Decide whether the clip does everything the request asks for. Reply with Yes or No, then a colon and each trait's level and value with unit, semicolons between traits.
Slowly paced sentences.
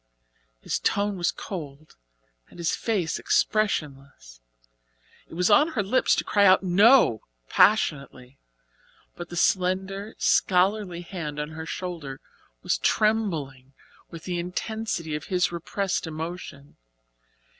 Yes: slow, 120 wpm